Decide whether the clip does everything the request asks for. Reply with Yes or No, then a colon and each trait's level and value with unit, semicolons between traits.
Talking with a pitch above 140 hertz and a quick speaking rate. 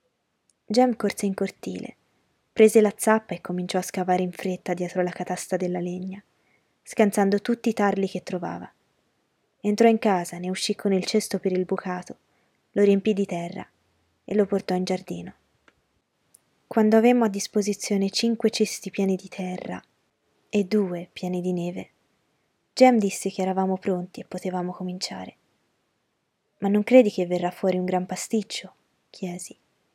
No: high, 190 Hz; average, 150 wpm